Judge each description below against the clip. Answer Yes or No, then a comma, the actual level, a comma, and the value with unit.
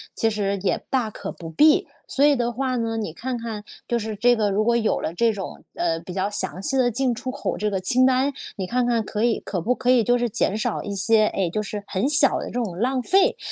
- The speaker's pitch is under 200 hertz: No, high, 225 Hz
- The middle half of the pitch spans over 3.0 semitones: Yes, average, 3.7 semitones